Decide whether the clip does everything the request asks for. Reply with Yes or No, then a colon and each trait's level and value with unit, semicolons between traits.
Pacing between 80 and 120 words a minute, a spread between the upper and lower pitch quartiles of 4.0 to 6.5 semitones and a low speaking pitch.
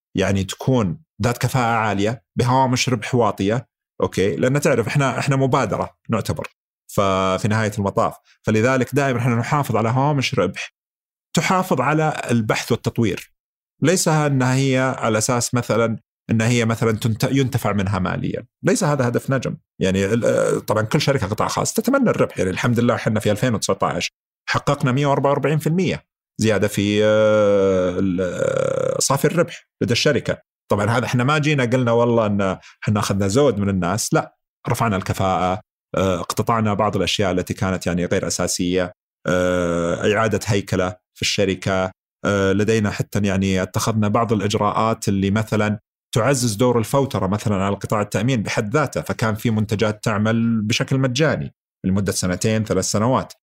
No: fast, 135 wpm; average, 4.5 semitones; low, 110 Hz